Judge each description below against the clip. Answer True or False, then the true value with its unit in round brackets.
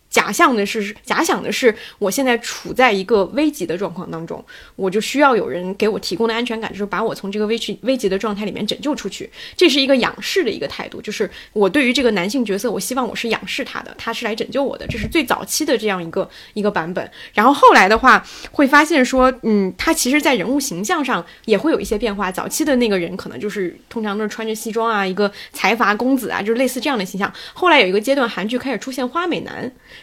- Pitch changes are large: False (4.6 semitones)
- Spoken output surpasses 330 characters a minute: True (370 characters per minute)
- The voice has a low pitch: False (225 Hz)